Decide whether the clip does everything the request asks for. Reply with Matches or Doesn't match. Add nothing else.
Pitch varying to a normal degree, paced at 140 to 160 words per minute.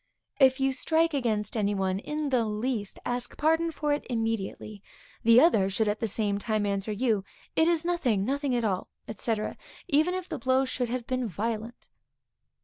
Doesn't match